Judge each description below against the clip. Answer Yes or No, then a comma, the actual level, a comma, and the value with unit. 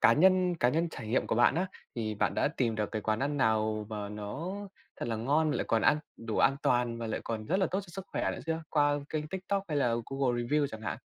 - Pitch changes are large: Yes, wide, 6.2 semitones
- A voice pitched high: No, low, 130 Hz